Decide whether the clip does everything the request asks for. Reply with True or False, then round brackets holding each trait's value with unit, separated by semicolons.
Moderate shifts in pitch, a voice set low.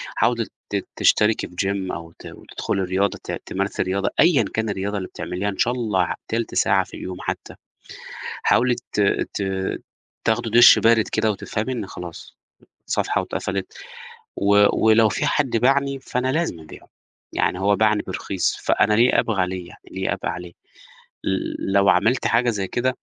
True (3.6 semitones; 100 Hz)